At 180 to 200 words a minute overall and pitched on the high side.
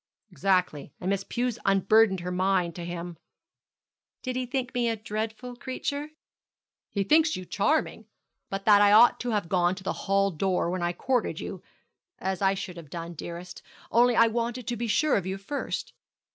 Yes: average, 185 wpm; high, 200 Hz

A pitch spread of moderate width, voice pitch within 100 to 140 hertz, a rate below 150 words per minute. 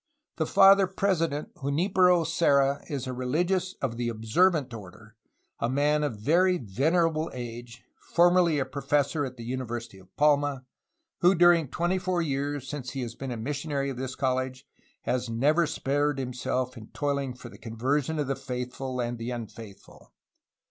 No: average, 4.4 semitones; low, 135 Hz; average, 160 wpm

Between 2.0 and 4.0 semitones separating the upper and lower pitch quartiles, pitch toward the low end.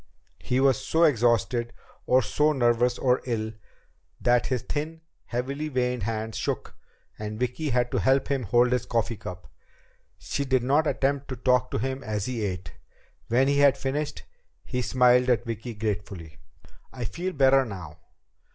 Yes: average, 3.0 semitones; low, 125 Hz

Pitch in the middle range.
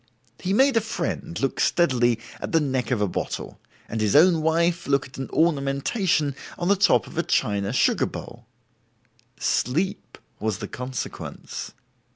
Yes: medium, 145 Hz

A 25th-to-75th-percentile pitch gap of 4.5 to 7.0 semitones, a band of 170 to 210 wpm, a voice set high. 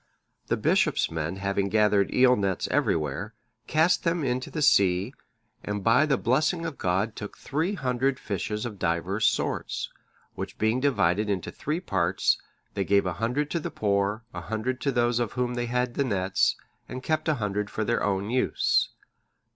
No: average, 4.8 semitones; average, 175 wpm; low, 110 Hz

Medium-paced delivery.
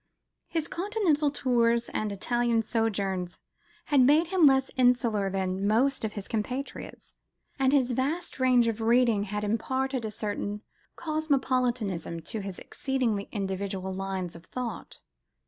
No: slow, 130 wpm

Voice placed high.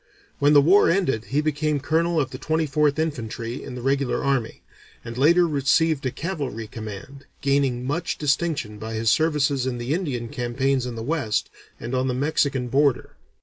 No: medium, 140 Hz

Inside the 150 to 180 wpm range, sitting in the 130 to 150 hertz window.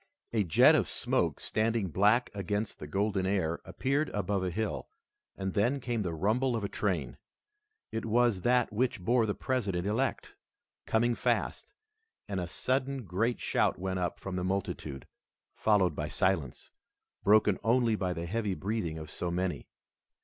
No: average, 160 wpm; low, 100 Hz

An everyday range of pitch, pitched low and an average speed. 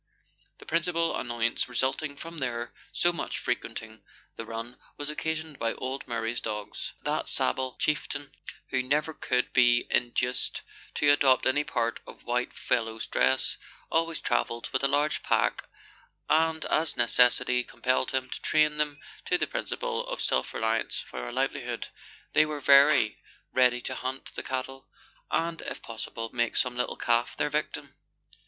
Yes: average, 4.1 semitones; low, 130 Hz; average, 155 wpm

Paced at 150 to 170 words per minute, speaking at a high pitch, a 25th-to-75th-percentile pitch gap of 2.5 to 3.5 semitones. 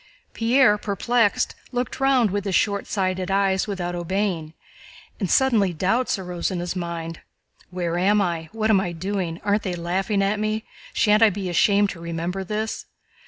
Yes: average, 165 wpm; high, 195 Hz; average, 3.1 semitones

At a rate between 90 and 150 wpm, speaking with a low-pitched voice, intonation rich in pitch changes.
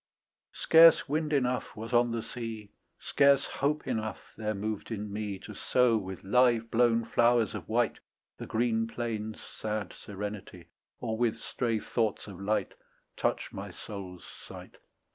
No: average, 145 wpm; low, 110 Hz; narrow, 2.5 semitones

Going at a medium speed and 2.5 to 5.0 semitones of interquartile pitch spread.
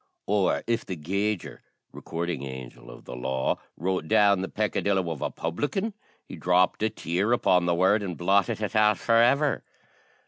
Yes: average, 170 wpm; average, 4.1 semitones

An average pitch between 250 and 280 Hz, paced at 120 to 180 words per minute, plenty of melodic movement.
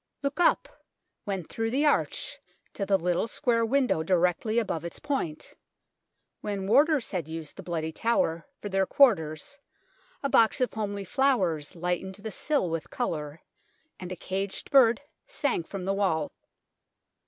No: high, 195 Hz; average, 150 wpm; wide, 6.2 semitones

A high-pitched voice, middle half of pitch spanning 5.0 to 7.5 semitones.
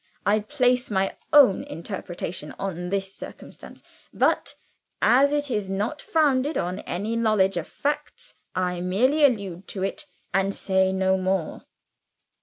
Yes: high, 195 Hz; average, 5.3 semitones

